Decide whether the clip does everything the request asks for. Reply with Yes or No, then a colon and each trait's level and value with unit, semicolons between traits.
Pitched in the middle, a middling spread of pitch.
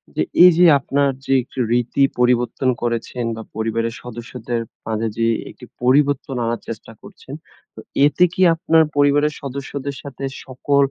No: low, 130 Hz; average, 3.3 semitones